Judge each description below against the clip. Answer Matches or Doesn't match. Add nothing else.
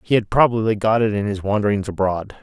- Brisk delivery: Matches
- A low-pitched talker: Matches